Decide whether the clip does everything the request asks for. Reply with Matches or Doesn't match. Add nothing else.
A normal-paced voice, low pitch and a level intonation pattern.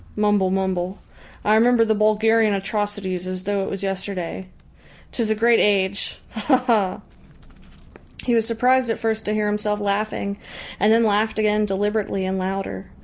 Doesn't match